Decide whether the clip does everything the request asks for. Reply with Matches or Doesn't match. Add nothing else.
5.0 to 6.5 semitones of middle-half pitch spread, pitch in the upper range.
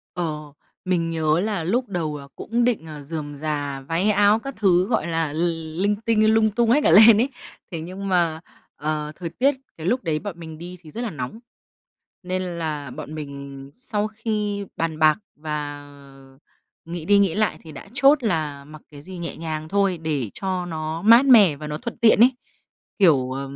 Doesn't match